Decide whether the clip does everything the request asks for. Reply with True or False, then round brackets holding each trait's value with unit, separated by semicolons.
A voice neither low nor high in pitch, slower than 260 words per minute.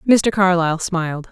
True (180 Hz; 135 wpm)